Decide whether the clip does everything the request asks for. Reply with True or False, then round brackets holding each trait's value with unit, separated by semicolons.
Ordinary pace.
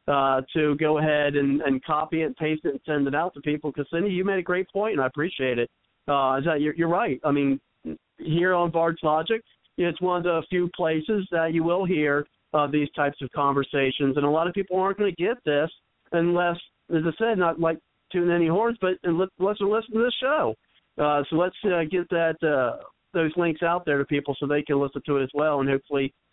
False (235 wpm)